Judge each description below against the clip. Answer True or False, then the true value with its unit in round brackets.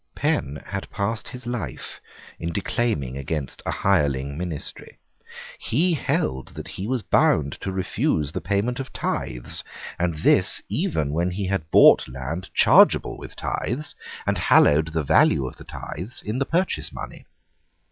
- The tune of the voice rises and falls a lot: True (6.9 semitones)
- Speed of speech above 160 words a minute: False (150 wpm)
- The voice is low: True (90 Hz)